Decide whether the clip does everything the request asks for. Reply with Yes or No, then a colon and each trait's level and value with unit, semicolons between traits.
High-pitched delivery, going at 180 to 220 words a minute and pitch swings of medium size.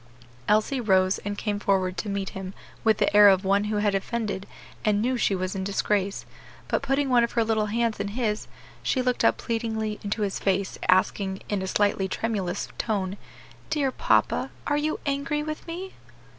Yes: high, 210 Hz; average, 185 wpm; average, 3.2 semitones